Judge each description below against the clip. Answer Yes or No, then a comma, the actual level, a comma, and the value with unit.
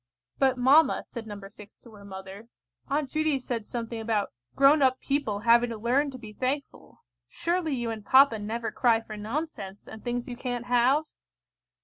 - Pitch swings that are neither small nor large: Yes, average, 3.7 semitones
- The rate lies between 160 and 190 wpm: Yes, average, 175 wpm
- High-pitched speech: Yes, high, 240 Hz